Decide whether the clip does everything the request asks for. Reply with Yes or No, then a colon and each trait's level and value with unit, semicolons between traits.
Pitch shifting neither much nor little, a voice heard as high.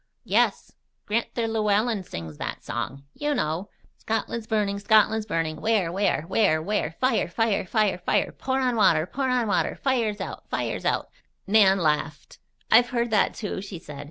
Yes: average, 4.2 semitones; high, 210 Hz